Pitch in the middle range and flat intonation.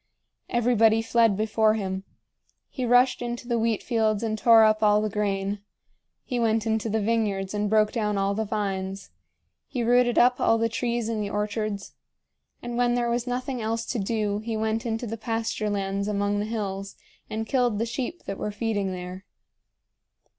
No: high, 220 Hz; narrow, 2.2 semitones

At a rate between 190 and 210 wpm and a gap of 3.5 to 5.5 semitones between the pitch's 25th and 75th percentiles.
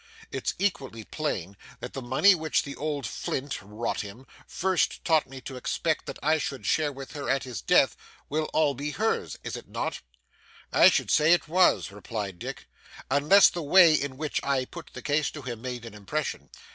Yes: average, 195 wpm; average, 3.9 semitones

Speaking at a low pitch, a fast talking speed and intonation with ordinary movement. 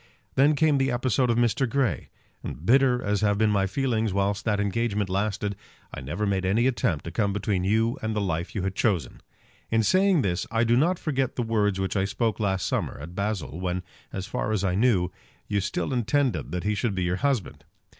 Yes: low, 105 Hz; fast, 215 wpm; average, 3.9 semitones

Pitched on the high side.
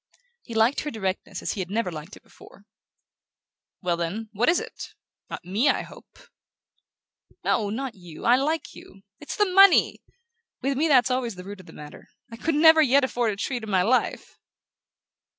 Yes: high, 230 Hz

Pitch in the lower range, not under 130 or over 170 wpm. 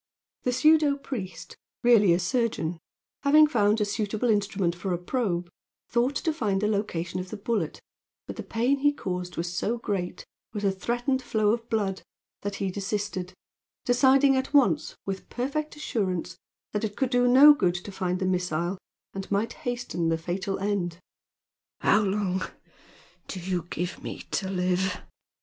No: high, 205 Hz; average, 165 wpm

